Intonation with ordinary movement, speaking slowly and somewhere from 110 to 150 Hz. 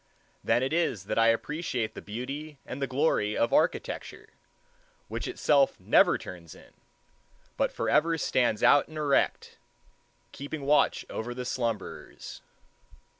Yes: average, 4.6 semitones; slow, 130 wpm; low, 135 Hz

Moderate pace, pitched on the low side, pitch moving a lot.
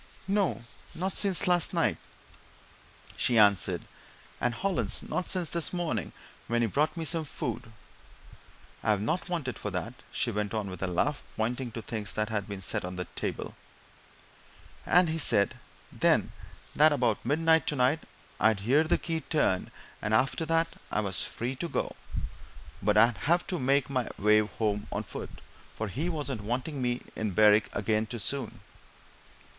Yes: average, 170 wpm; low, 120 Hz; wide, 7.0 semitones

